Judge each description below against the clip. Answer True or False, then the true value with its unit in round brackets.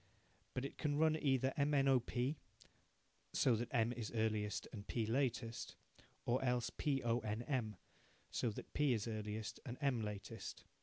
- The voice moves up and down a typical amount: True (3.5 semitones)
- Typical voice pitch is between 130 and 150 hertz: False (120 Hz)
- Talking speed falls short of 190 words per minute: True (170 wpm)